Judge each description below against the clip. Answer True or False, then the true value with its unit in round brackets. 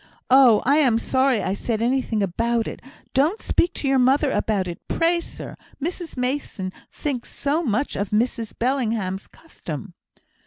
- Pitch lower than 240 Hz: False (250 Hz)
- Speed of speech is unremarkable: True (155 wpm)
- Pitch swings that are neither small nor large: True (4.7 semitones)